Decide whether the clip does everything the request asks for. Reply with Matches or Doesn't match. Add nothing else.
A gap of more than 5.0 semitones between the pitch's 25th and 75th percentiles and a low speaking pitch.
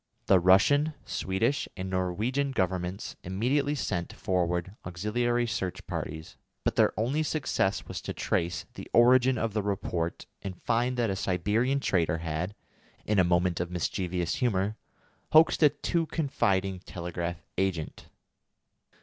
Matches